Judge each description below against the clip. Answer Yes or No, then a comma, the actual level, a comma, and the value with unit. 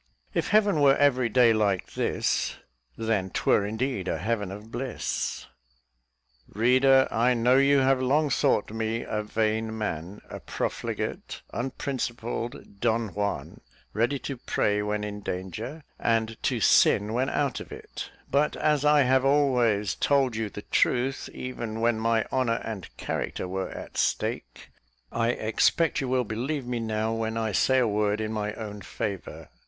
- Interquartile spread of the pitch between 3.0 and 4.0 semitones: Yes, average, 3.5 semitones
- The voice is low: Yes, low, 115 Hz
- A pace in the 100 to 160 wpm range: Yes, average, 155 wpm